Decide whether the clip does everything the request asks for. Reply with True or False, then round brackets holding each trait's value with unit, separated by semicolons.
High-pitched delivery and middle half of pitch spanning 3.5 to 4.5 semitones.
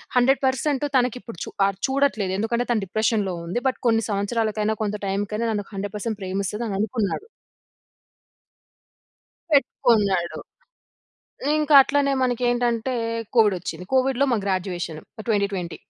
True (220 Hz; 3.9 semitones)